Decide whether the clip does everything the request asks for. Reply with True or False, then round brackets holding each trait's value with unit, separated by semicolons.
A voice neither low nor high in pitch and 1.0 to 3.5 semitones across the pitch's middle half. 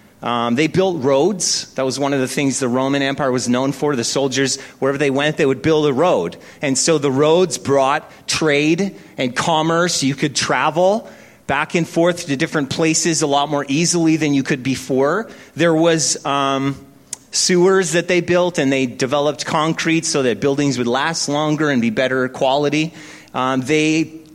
True (145 Hz; 3.1 semitones)